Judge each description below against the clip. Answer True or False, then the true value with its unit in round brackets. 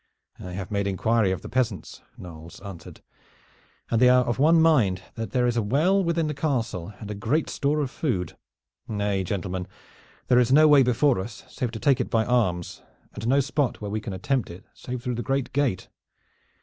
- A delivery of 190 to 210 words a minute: True (200 wpm)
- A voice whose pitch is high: False (120 Hz)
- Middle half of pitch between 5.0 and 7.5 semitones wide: True (5.4 semitones)